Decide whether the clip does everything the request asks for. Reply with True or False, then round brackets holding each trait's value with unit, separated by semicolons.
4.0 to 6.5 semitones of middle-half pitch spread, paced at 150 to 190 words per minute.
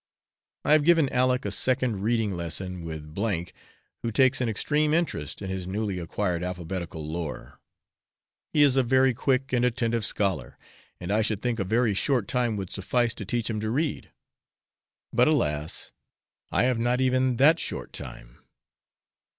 True (5.6 semitones; 165 wpm)